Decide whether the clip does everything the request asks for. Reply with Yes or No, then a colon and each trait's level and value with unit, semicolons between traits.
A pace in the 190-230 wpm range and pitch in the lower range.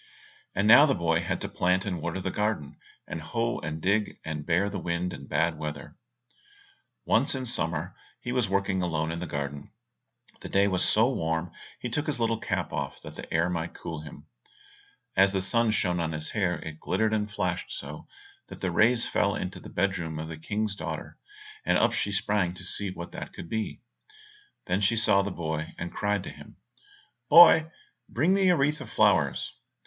Yes: average, 200 wpm; very low, 95 Hz